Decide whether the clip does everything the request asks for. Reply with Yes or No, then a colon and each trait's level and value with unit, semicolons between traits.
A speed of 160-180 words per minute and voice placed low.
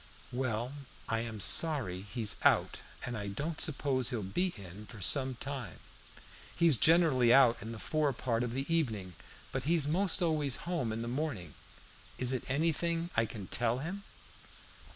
Yes: average, 165 wpm; low, 130 Hz